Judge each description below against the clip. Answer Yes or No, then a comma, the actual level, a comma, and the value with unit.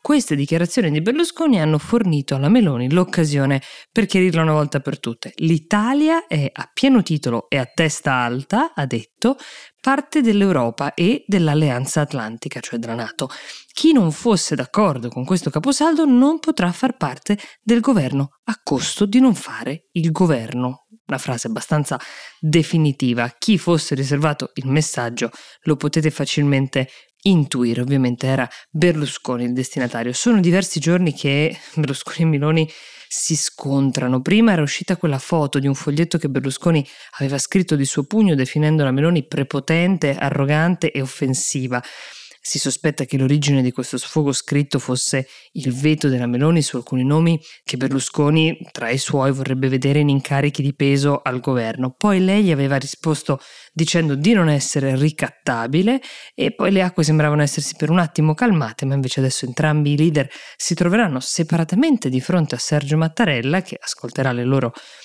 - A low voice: No, medium, 150 Hz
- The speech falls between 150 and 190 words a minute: Yes, average, 155 wpm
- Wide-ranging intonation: No, average, 4.6 semitones